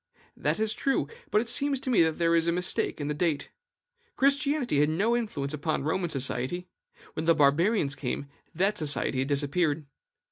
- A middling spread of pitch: No, wide, 6.6 semitones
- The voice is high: No, medium, 165 Hz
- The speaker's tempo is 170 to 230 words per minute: Yes, average, 180 wpm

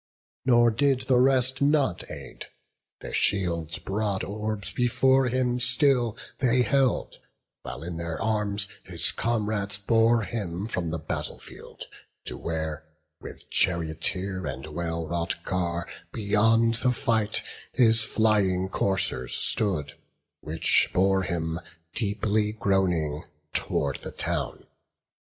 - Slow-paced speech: Yes, slow, 120 wpm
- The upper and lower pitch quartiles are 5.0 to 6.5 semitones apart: Yes, wide, 5.4 semitones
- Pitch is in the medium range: No, low, 105 Hz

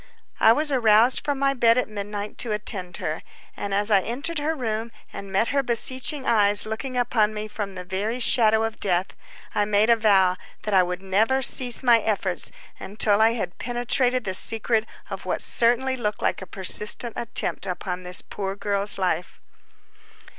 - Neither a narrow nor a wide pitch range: Yes, average, 3.4 semitones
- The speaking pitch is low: No, high, 215 Hz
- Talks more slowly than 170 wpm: No, average, 180 wpm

